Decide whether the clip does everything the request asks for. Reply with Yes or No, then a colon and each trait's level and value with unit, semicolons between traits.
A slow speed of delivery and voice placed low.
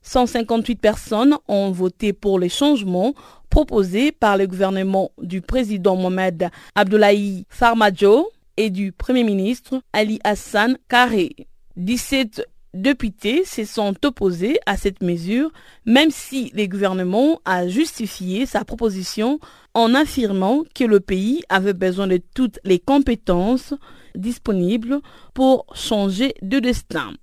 No: slow, 120 wpm; high, 215 Hz